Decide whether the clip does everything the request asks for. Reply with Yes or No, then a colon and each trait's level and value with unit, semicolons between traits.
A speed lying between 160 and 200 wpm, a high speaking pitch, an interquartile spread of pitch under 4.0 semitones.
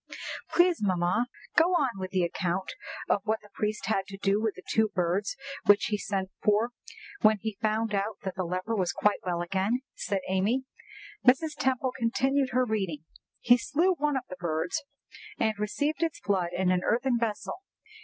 No: average, 175 wpm; high, 210 Hz; average, 4.8 semitones